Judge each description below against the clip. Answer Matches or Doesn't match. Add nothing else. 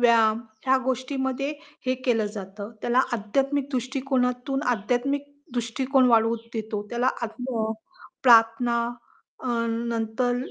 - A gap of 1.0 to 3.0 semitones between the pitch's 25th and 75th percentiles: Matches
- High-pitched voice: Matches